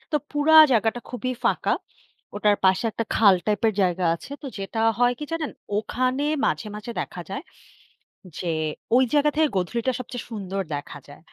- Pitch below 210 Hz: No, high, 230 Hz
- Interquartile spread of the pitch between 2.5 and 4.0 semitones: No, average, 4.6 semitones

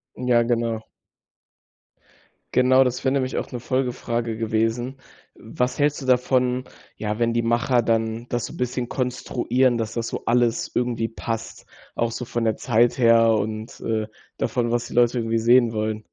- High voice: No, low, 120 Hz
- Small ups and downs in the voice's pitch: Yes, narrow, 1.7 semitones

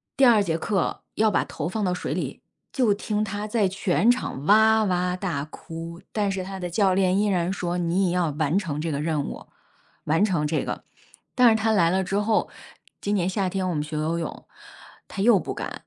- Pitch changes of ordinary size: Yes, average, 3.7 semitones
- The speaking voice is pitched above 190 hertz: No, medium, 185 Hz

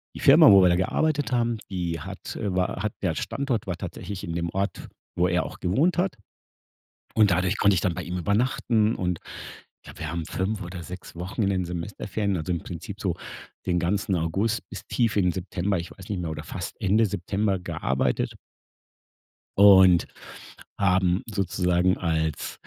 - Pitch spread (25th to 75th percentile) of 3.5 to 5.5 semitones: No, narrow, 2.6 semitones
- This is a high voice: No, very low, 95 Hz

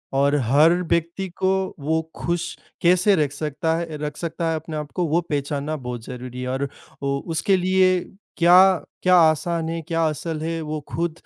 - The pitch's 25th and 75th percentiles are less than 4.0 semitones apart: Yes, average, 2.8 semitones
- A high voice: No, medium, 160 Hz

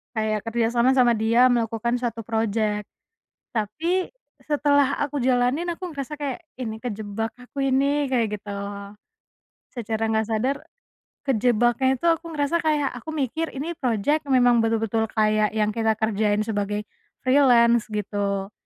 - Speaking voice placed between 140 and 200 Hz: No, high, 235 Hz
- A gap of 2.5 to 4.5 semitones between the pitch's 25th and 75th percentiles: Yes, average, 4.1 semitones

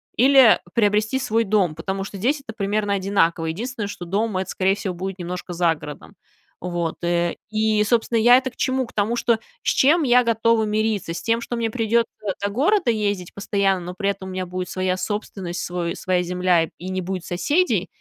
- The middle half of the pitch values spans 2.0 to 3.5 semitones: No, average, 4.0 semitones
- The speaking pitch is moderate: No, high, 200 Hz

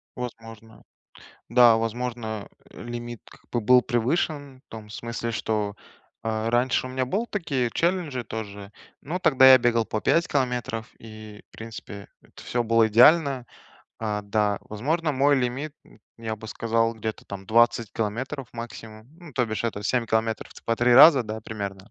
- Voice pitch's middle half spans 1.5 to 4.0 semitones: Yes, average, 2.7 semitones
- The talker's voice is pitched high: No, low, 115 Hz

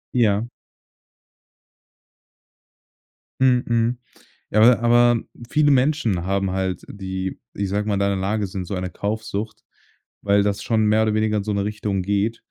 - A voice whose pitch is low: Yes, low, 105 Hz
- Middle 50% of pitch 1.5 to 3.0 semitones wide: Yes, narrow, 2.6 semitones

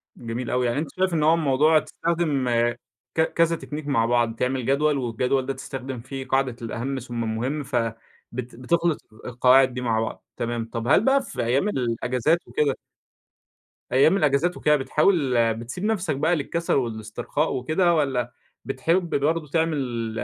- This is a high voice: No, low, 135 Hz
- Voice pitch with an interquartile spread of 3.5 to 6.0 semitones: Yes, average, 4.5 semitones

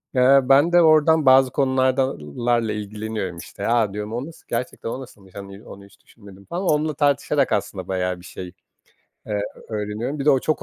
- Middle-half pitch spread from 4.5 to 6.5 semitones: Yes, wide, 5.4 semitones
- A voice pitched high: No, low, 120 Hz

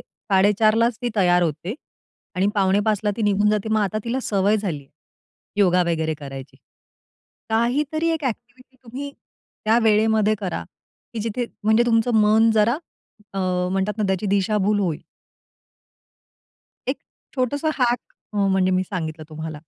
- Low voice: No, high, 210 Hz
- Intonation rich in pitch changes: No, average, 3.4 semitones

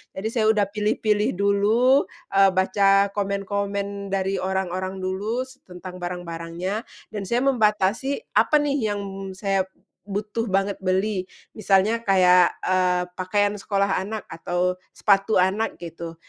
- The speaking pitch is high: Yes, high, 195 Hz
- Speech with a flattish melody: Yes, narrow, 2.1 semitones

